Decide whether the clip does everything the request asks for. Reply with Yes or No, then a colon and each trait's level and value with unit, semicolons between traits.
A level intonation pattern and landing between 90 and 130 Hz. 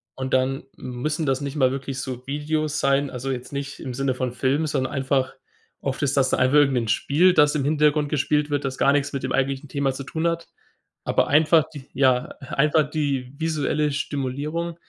No: narrow, 2.2 semitones; medium, 140 Hz